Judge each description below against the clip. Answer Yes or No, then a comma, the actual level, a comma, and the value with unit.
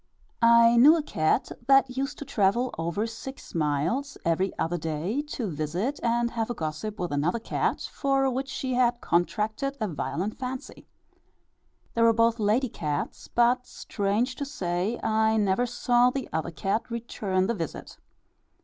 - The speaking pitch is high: Yes, high, 230 Hz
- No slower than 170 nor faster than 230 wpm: No, average, 160 wpm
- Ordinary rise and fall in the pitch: No, wide, 5.7 semitones